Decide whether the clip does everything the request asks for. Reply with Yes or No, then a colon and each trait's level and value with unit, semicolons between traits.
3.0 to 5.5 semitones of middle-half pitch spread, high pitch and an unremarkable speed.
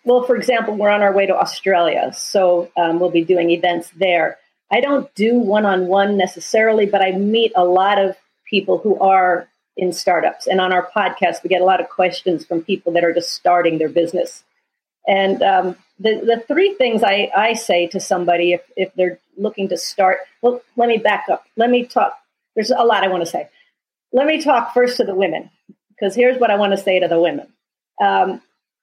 No: average, 4.1 semitones; high, 195 Hz; fast, 210 wpm